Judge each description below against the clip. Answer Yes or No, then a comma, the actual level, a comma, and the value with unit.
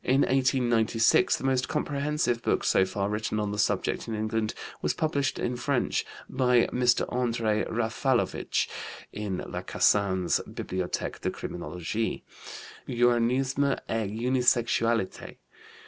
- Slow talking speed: Yes, slow, 115 wpm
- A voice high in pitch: No, low, 120 Hz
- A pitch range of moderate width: Yes, average, 3.0 semitones